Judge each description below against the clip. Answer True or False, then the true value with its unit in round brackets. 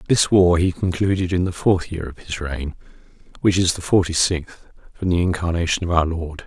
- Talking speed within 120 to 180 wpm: False (205 wpm)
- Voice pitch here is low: True (85 Hz)